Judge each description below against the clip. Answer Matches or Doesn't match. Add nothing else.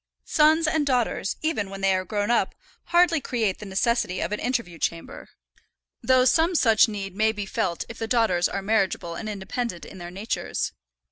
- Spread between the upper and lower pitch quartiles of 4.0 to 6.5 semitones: Matches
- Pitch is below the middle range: Doesn't match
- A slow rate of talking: Doesn't match